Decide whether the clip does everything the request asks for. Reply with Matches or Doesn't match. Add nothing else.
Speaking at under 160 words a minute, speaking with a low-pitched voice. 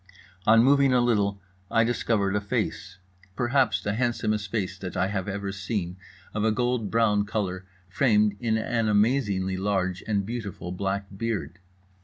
Matches